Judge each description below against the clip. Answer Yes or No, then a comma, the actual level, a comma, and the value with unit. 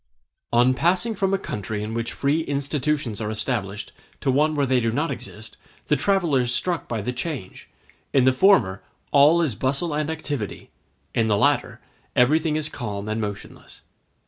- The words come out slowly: No, average, 170 wpm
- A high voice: No, low, 130 Hz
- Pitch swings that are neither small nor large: No, wide, 5.8 semitones